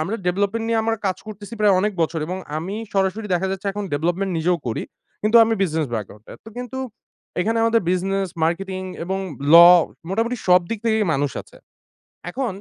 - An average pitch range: Yes, average, 3.9 semitones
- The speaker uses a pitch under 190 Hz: No, high, 195 Hz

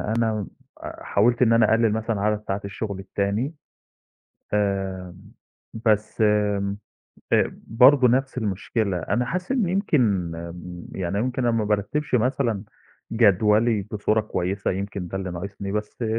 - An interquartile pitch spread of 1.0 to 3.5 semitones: Yes, average, 3.0 semitones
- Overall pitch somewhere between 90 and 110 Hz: Yes, low, 105 Hz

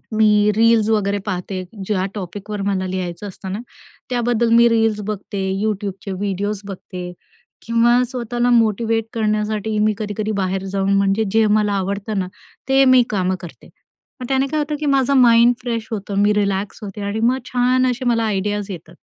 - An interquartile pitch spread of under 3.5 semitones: Yes, average, 2.8 semitones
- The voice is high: Yes, high, 210 Hz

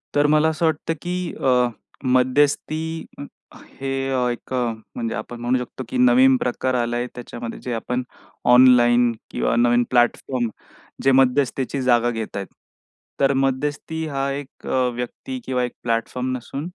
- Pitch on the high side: No, low, 130 Hz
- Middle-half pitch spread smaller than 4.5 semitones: Yes, narrow, 2.4 semitones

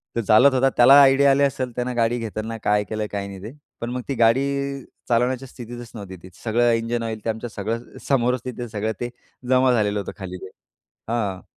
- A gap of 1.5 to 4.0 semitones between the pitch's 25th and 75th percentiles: Yes, average, 2.8 semitones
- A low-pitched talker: Yes, low, 115 Hz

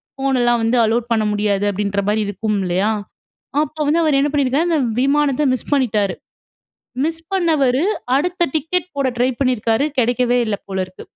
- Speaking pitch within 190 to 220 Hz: No, very high, 250 Hz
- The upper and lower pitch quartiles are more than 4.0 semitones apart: Yes, wide, 5.4 semitones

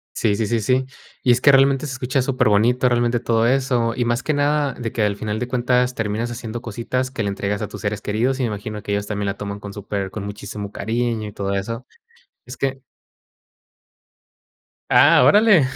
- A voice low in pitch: Yes, low, 115 Hz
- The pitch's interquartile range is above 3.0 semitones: Yes, average, 3.7 semitones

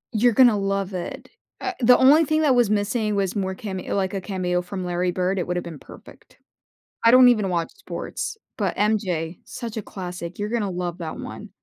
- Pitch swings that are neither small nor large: Yes, average, 3.8 semitones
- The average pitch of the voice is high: Yes, high, 195 Hz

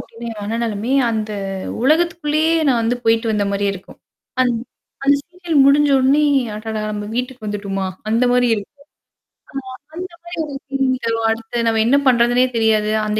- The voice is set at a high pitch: Yes, high, 235 Hz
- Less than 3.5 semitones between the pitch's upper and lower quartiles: No, average, 4.3 semitones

